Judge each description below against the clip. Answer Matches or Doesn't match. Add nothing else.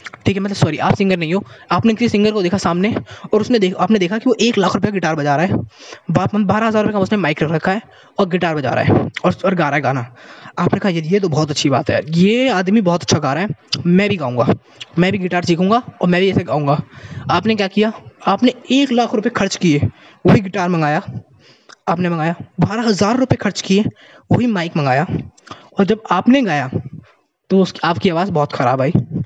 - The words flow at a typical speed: Doesn't match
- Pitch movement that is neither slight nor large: Matches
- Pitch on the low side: Doesn't match